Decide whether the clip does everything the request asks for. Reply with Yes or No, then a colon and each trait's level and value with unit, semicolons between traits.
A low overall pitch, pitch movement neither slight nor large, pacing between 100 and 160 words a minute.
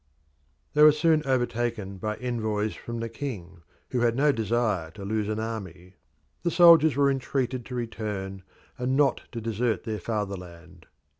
Yes: low, 115 Hz; average, 4.2 semitones; average, 155 wpm